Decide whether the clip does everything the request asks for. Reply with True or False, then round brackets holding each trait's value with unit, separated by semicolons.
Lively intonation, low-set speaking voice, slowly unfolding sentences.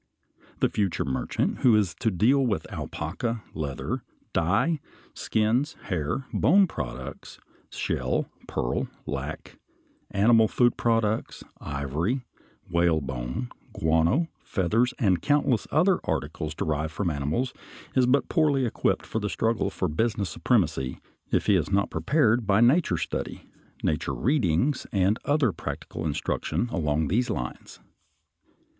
True (7.8 semitones; 105 Hz; 125 wpm)